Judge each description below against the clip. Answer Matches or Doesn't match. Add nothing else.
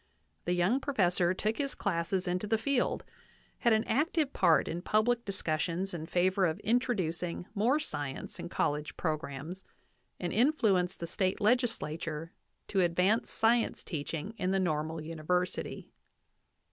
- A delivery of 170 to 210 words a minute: Doesn't match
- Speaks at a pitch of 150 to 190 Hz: Matches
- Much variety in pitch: Doesn't match